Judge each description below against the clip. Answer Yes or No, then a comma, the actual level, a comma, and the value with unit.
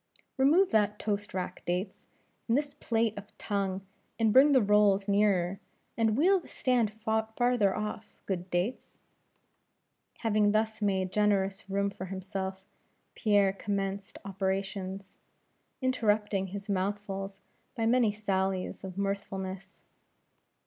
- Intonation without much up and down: Yes, narrow, 2.2 semitones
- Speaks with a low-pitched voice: No, high, 200 Hz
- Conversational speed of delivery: No, slow, 120 wpm